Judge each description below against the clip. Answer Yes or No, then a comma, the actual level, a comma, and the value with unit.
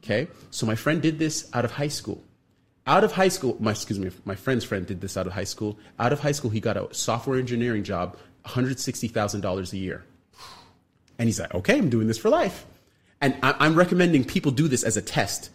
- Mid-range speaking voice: No, low, 115 Hz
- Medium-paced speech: No, fast, 220 wpm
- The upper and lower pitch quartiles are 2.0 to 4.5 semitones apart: No, average, 5.2 semitones